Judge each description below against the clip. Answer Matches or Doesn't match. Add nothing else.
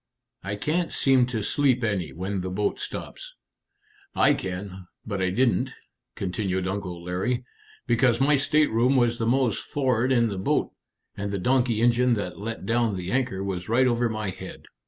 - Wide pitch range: Doesn't match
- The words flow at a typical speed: Matches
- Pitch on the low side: Matches